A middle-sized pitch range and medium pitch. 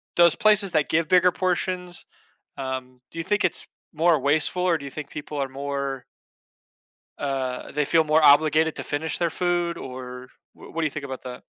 Yes: average, 4.0 semitones; medium, 155 Hz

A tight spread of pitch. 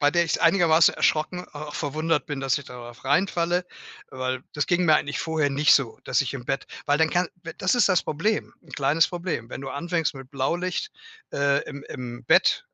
No: average, 4.0 semitones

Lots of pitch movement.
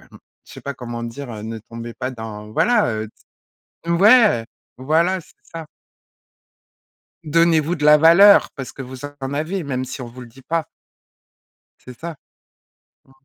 Yes: wide, 5.7 semitones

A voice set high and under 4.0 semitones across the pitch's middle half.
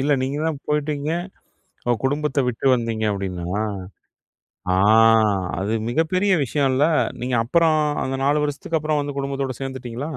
No: medium, 140 Hz; average, 3.3 semitones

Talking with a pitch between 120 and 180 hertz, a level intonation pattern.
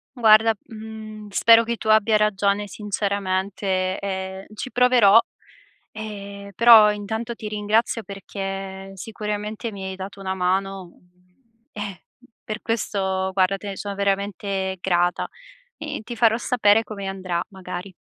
No: high, 200 Hz; narrow, 2.1 semitones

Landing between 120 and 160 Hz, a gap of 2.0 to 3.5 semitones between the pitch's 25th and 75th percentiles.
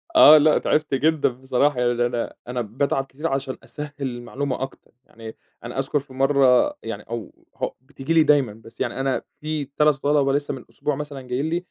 Yes: low, 135 Hz; average, 2.9 semitones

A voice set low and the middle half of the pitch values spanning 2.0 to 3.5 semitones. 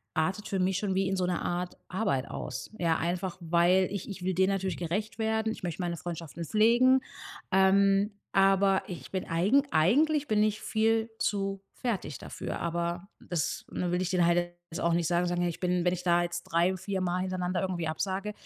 No: medium, 185 Hz; narrow, 2.4 semitones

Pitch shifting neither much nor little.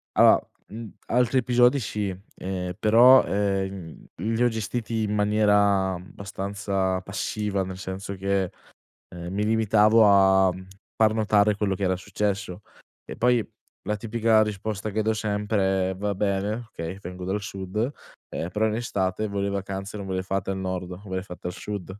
No: narrow, 2.2 semitones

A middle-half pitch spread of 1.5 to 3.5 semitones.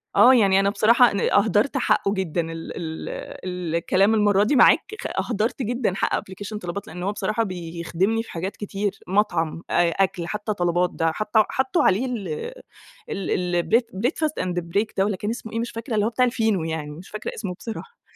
No: average, 4.2 semitones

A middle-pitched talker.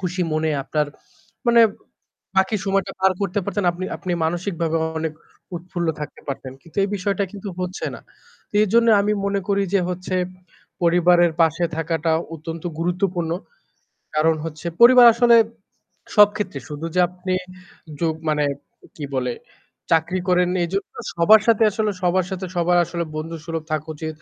Yes: medium, 175 Hz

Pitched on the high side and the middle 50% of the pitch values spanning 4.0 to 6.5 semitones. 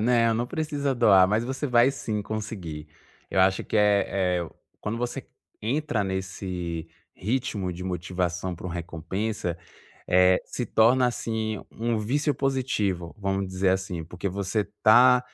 No: low, 105 Hz; average, 4.4 semitones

